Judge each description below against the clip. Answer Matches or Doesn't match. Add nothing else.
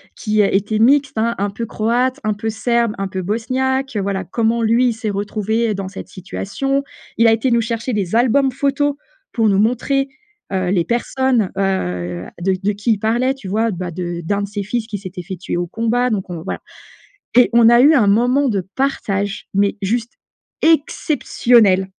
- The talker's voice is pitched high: Matches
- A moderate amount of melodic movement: Matches